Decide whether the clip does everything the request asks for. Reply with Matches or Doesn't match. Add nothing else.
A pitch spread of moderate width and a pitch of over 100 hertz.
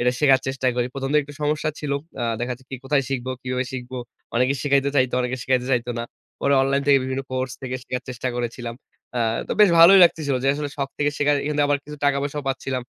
Doesn't match